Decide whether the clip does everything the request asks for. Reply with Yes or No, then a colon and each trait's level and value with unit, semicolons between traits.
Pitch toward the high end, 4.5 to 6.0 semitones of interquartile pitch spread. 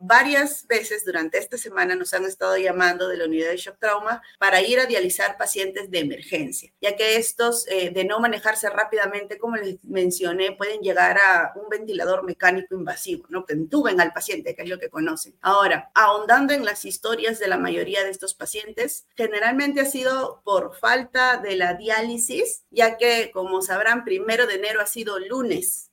Yes: high, 220 Hz; average, 5.3 semitones